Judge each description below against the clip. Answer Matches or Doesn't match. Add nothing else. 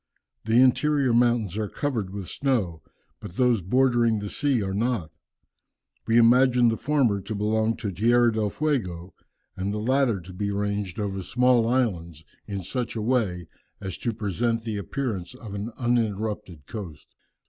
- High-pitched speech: Doesn't match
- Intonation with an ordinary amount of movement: Matches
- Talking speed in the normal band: Matches